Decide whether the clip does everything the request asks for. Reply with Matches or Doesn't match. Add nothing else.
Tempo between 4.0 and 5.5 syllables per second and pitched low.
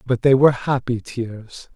Matches